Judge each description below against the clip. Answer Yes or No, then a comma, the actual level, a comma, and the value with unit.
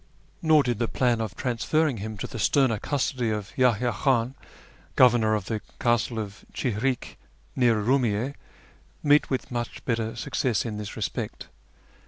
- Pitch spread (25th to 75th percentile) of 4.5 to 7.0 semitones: No, average, 3.0 semitones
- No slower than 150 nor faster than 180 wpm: Yes, average, 155 wpm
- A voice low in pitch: Yes, low, 120 Hz